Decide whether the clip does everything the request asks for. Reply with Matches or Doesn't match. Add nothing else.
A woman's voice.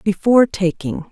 Matches